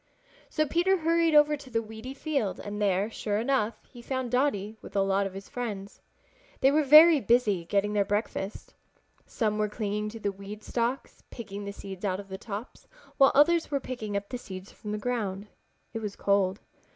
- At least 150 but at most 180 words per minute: No, average, 195 wpm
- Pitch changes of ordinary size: Yes, average, 4.6 semitones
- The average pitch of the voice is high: Yes, high, 215 Hz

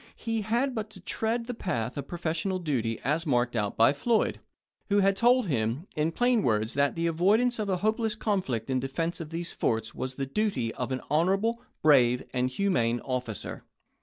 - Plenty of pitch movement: Yes, wide, 8.9 semitones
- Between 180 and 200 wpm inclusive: Yes, average, 190 wpm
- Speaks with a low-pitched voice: No, medium, 165 Hz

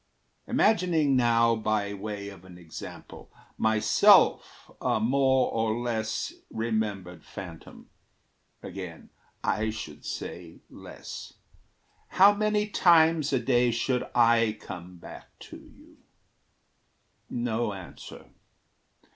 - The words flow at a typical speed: No, slow, 100 wpm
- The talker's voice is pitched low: Yes, low, 110 Hz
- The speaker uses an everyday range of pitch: Yes, average, 4.2 semitones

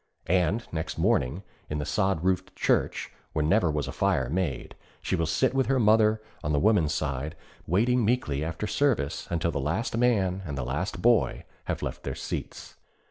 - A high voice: No, very low, 90 Hz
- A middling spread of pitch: No, wide, 6.3 semitones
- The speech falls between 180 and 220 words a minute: Yes, average, 185 wpm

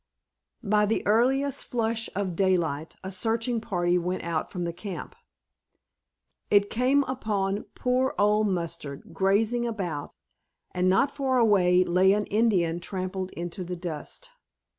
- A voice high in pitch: Yes, high, 195 Hz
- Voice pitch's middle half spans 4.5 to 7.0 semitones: No, average, 4.1 semitones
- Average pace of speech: No, slow, 130 wpm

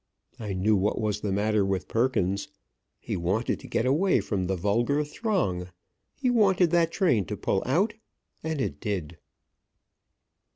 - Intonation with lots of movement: Yes, wide, 8.6 semitones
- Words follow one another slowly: No, average, 155 wpm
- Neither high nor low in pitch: No, low, 110 Hz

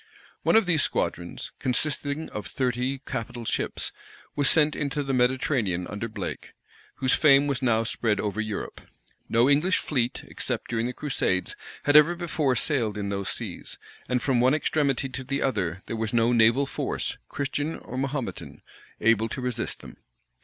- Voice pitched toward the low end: Yes, low, 125 Hz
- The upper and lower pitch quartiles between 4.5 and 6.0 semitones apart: No, average, 4.0 semitones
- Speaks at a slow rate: No, average, 165 wpm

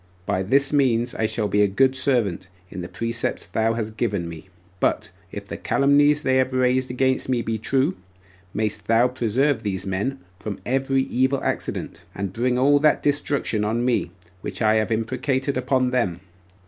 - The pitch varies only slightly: No, average, 3.8 semitones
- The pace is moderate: Yes, average, 180 wpm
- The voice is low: Yes, low, 120 Hz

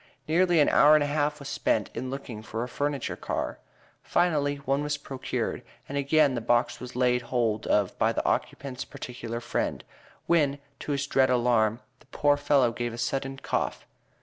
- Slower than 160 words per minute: No, average, 185 wpm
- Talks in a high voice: No, low, 135 Hz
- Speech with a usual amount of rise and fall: Yes, average, 3.2 semitones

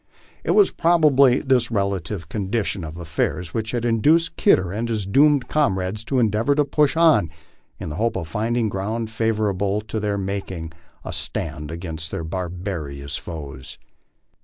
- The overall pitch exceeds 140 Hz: No, low, 105 Hz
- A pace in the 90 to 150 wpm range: No, average, 160 wpm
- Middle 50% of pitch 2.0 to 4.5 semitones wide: No, wide, 5.4 semitones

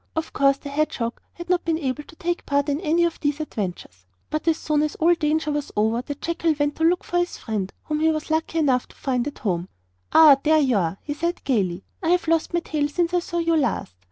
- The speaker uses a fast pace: Yes, fast, 245 wpm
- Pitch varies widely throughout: No, average, 3.7 semitones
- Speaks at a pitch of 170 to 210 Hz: No, very high, 300 Hz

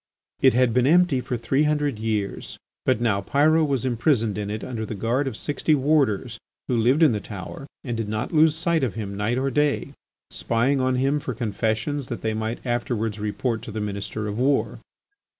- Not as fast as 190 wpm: No, average, 200 wpm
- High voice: No, low, 120 Hz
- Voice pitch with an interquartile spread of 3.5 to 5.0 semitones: Yes, average, 4.3 semitones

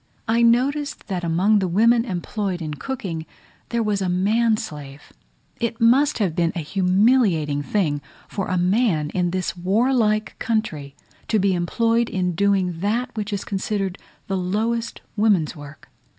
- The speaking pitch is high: Yes, high, 195 Hz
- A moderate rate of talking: Yes, average, 150 wpm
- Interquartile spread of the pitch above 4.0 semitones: Yes, average, 4.6 semitones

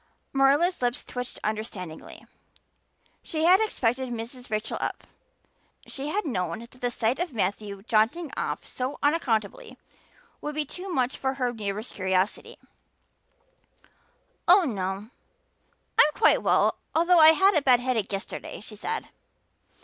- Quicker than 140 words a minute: No, slow, 135 wpm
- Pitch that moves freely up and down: Yes, wide, 6.4 semitones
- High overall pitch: Yes, very high, 250 Hz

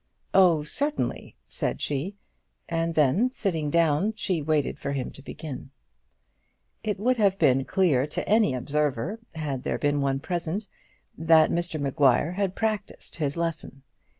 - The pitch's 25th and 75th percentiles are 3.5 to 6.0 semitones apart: Yes, average, 5.1 semitones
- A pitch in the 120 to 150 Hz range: No, medium, 160 Hz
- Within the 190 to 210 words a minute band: No, average, 145 wpm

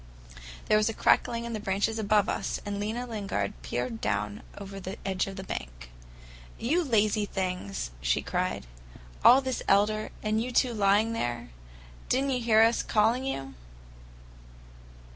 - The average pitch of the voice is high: Yes, high, 210 Hz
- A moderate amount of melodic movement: Yes, average, 3.8 semitones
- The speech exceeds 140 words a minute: Yes, average, 160 wpm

